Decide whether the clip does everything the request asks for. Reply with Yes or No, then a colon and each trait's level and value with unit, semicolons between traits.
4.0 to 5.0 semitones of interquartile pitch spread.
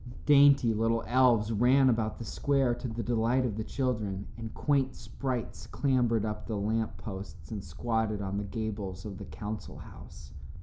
No: average, 3.0 semitones